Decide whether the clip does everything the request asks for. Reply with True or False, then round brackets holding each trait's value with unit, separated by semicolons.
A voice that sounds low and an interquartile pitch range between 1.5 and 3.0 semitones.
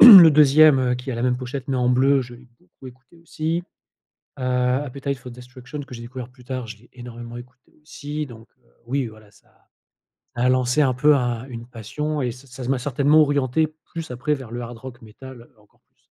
True (125 Hz; 2.6 semitones)